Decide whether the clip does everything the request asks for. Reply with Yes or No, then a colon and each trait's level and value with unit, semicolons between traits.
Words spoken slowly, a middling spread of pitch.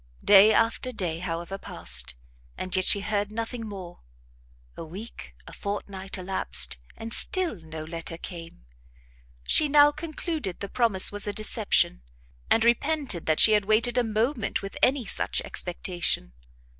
No: average, 145 wpm; average, 4.4 semitones